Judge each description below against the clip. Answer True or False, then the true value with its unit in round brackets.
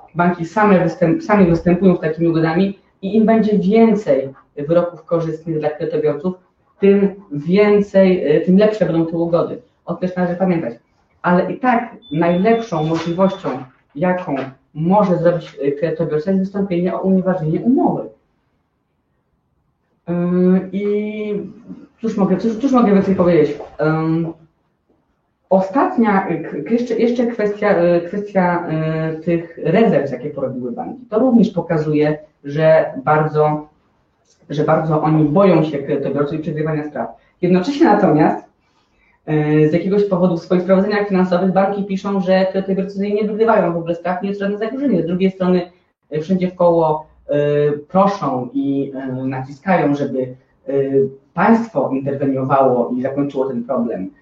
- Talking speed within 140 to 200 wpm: False (120 wpm)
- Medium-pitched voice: True (175 Hz)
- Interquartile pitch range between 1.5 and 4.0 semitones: False (4.4 semitones)